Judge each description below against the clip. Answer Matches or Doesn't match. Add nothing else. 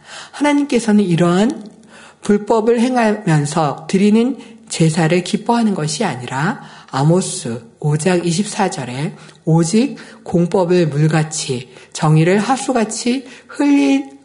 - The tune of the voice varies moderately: Doesn't match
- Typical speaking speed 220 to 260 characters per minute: Matches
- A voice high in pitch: Matches